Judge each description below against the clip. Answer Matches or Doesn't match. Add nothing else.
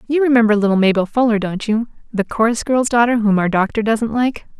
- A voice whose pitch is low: Doesn't match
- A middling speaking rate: Matches